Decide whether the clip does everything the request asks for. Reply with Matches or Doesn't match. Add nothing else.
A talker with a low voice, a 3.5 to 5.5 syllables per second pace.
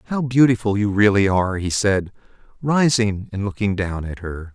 Matches